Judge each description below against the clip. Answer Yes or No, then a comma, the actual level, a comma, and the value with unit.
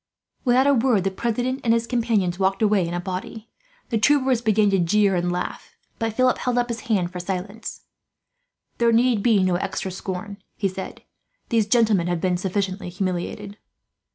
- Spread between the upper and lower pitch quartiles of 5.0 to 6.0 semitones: No, average, 3.9 semitones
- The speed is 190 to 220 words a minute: No, average, 180 wpm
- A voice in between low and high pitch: No, high, 205 Hz